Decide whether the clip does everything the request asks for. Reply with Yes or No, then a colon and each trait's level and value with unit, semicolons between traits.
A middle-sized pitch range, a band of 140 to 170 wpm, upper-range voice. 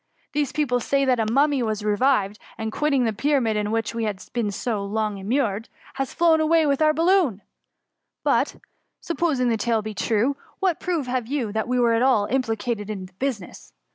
No: average, 4.5 semitones; average, 200 wpm; high, 240 Hz